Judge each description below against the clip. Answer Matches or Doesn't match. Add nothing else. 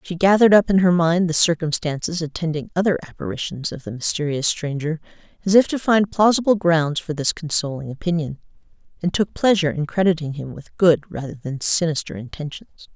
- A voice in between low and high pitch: Matches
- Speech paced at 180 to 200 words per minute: Doesn't match